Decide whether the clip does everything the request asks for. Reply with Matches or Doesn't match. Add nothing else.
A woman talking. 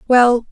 Matches